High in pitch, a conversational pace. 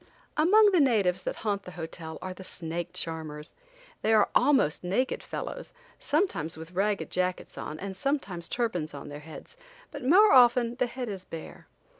Yes: high, 195 Hz; average, 170 wpm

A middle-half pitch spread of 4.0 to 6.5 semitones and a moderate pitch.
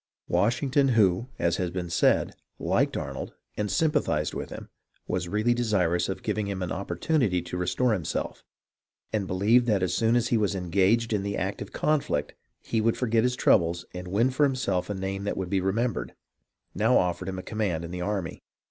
No: average, 4.5 semitones; low, 100 Hz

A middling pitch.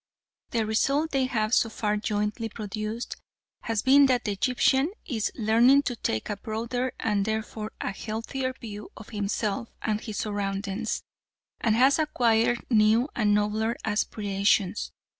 No: high, 220 Hz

